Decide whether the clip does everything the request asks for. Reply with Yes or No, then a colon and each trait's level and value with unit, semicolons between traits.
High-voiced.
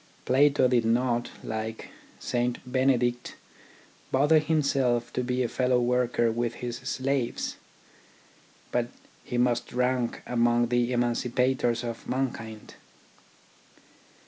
No: low, 125 Hz